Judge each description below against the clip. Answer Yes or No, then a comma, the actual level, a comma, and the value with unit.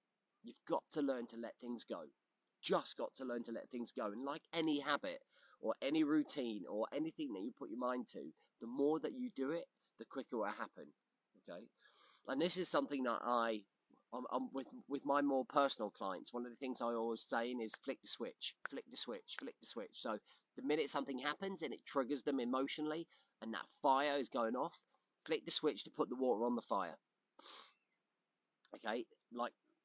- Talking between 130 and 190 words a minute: No, fast, 205 wpm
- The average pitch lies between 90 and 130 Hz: No, medium, 140 Hz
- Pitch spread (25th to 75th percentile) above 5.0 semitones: Yes, wide, 5.5 semitones